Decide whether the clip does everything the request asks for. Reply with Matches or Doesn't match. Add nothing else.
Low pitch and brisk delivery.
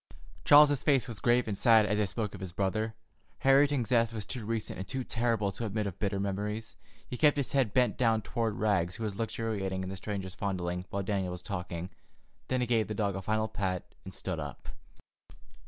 Matches